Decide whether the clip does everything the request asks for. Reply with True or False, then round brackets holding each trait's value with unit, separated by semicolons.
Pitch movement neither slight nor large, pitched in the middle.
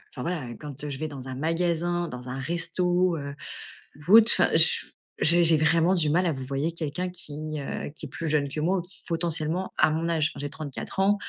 True (3.1 semitones; 160 Hz)